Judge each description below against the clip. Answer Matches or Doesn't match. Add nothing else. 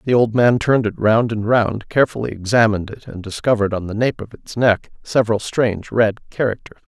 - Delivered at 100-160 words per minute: Doesn't match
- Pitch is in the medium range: Doesn't match